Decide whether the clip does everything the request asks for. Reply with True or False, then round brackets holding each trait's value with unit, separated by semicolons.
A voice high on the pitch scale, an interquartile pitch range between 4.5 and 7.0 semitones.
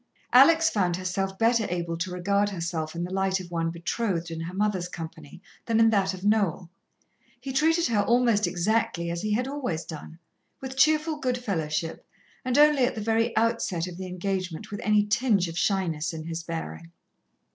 True (195 Hz; 5.1 semitones)